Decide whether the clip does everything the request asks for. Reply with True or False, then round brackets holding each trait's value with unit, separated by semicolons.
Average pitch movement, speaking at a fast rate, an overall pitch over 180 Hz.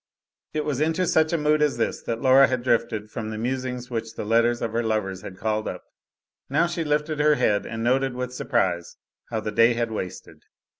False (4.4 semitones; 210 wpm; 120 Hz)